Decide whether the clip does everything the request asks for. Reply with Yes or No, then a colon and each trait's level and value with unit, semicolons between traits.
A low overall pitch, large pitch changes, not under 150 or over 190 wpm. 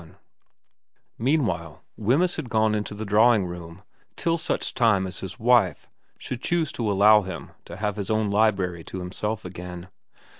No: low, 105 Hz; average, 3.8 semitones; average, 160 wpm